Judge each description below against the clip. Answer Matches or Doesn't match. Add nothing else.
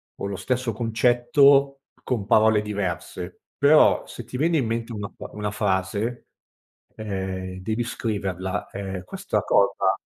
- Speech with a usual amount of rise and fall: Matches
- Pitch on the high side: Doesn't match